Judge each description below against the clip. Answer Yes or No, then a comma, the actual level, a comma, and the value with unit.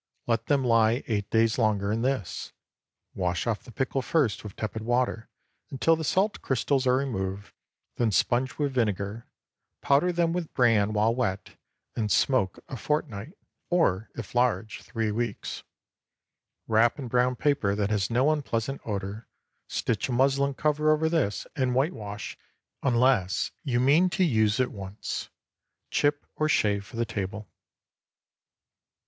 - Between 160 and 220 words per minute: No, average, 145 wpm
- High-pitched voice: No, low, 120 Hz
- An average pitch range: Yes, average, 4.5 semitones